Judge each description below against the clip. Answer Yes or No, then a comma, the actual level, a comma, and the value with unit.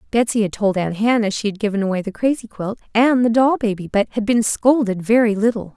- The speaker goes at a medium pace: No, fast, 230 wpm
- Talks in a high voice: Yes, high, 220 Hz